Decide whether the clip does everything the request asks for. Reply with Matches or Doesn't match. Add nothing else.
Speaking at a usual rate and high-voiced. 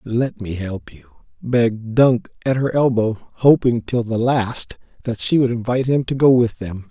Doesn't match